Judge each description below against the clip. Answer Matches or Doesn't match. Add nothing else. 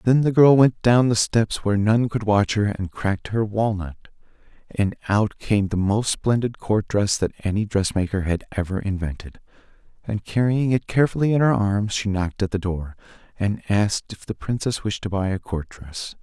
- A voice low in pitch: Matches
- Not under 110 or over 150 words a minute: Doesn't match